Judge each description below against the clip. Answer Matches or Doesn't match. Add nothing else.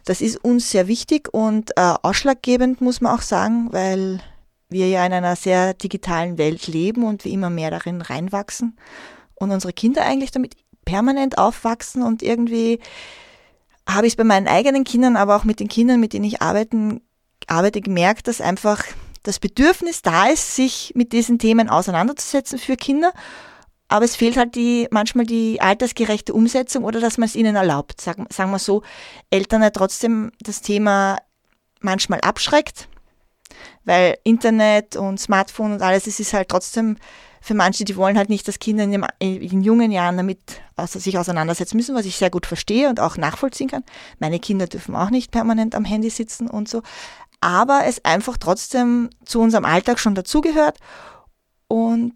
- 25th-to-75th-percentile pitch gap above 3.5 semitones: Matches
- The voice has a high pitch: Matches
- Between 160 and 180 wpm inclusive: Matches